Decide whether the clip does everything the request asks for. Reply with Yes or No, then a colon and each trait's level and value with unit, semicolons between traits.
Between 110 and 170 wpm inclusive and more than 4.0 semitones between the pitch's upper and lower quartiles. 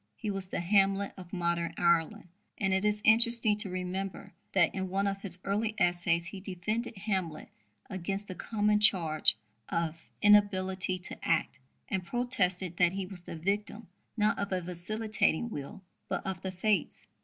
No: average, 165 wpm; average, 2.9 semitones